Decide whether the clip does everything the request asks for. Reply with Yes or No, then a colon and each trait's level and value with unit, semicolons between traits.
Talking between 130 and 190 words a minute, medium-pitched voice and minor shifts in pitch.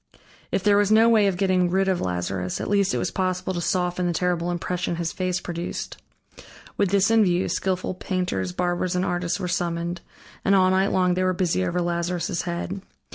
No: average, 200 wpm; medium, 180 Hz; narrow, 1.5 semitones